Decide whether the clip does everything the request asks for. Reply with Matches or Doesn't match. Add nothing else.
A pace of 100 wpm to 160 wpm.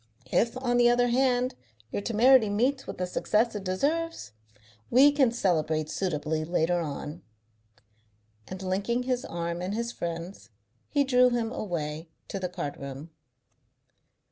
Matches